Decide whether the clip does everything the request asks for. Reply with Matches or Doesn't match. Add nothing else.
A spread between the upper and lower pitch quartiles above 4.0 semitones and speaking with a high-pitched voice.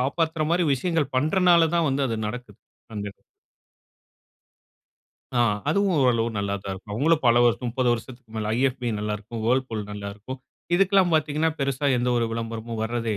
Doesn't match